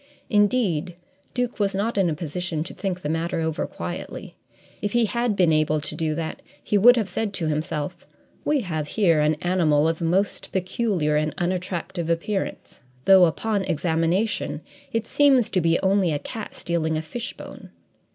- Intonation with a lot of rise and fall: No, average, 4.3 semitones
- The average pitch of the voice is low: No, medium, 180 Hz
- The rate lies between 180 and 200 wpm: No, average, 170 wpm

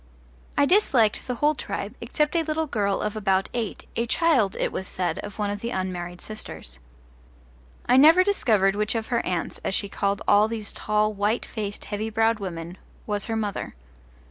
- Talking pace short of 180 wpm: No, average, 185 wpm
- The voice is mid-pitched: No, high, 210 Hz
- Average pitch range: Yes, average, 3.1 semitones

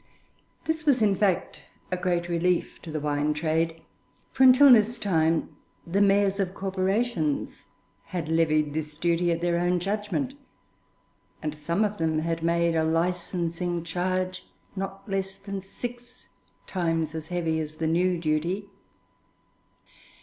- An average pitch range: Yes, average, 3.3 semitones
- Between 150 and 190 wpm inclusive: No, average, 140 wpm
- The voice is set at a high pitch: No, medium, 175 Hz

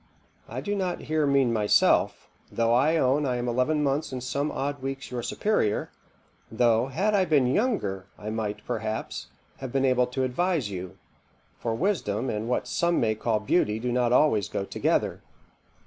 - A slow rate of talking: No, average, 175 wpm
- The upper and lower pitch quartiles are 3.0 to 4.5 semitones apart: No, average, 4.9 semitones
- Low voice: Yes, low, 125 Hz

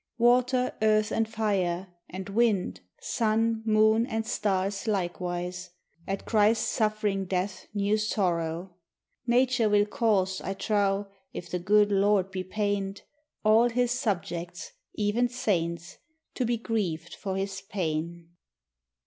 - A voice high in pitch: Yes, high, 205 Hz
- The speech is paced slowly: Yes, slow, 125 wpm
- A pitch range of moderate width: Yes, average, 3.1 semitones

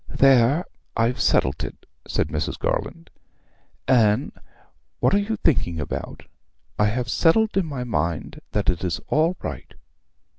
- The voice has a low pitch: Yes, low, 125 Hz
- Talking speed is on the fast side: No, average, 140 wpm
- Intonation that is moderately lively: No, wide, 7.8 semitones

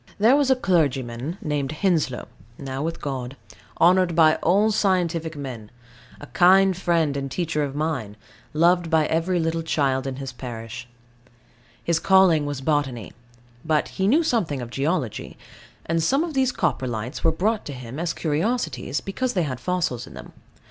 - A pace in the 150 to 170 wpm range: Yes, average, 160 wpm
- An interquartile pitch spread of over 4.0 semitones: Yes, average, 5.2 semitones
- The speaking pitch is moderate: Yes, medium, 160 Hz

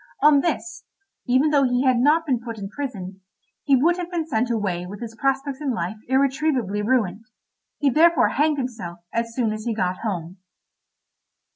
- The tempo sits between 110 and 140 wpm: No, average, 175 wpm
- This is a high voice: Yes, very high, 250 Hz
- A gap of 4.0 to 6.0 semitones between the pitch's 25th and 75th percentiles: Yes, average, 5.0 semitones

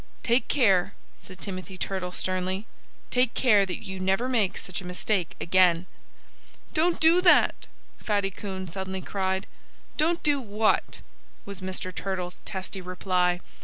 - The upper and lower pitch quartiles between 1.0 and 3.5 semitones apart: Yes, average, 2.7 semitones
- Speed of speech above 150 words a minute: No, average, 140 wpm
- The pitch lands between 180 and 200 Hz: Yes, high, 190 Hz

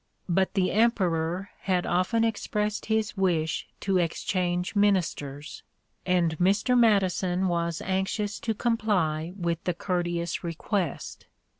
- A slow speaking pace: Yes, slow, 115 wpm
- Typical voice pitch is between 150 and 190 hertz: Yes, medium, 185 Hz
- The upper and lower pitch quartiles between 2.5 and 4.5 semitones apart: Yes, average, 3.2 semitones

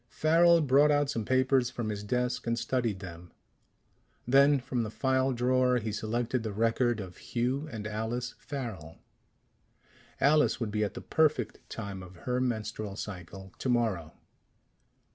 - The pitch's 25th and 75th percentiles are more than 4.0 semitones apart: No, average, 3.6 semitones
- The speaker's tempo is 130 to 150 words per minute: Yes, average, 145 wpm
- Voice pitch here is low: Yes, low, 120 Hz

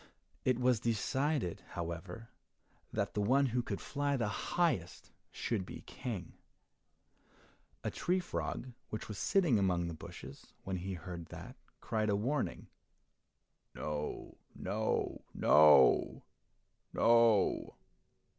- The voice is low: Yes, low, 110 Hz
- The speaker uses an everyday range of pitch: No, wide, 5.9 semitones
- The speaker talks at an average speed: No, slow, 115 wpm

